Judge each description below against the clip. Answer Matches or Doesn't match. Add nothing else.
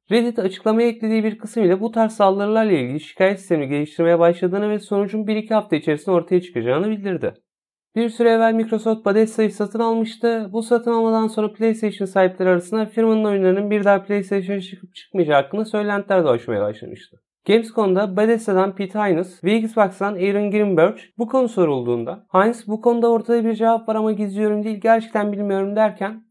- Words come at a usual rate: Doesn't match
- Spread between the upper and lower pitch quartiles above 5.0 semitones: Doesn't match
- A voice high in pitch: Matches